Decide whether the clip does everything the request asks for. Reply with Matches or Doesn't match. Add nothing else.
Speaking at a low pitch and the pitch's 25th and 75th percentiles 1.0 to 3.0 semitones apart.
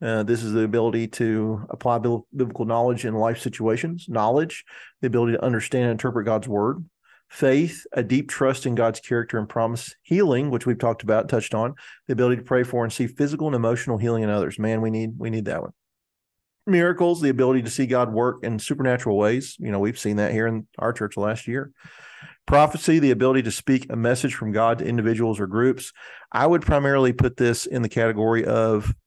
Matches